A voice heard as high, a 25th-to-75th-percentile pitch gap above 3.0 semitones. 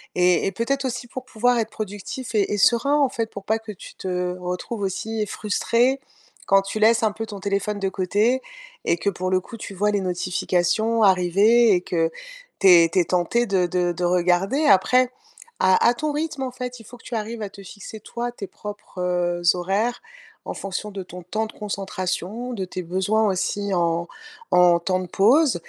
Yes: high, 200 Hz; average, 4.1 semitones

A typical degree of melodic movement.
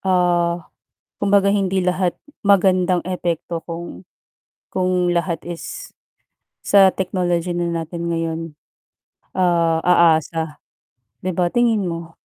No: narrow, 1.7 semitones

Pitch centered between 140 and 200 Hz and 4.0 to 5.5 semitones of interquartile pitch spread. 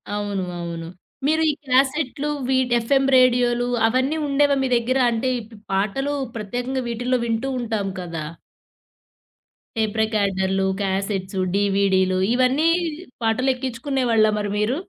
No: high, 235 Hz; average, 4.5 semitones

